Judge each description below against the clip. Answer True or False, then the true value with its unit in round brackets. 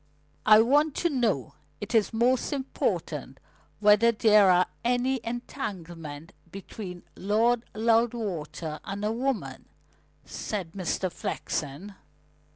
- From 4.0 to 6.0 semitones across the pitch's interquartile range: True (4.6 semitones)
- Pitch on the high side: True (215 Hz)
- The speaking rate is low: True (105 wpm)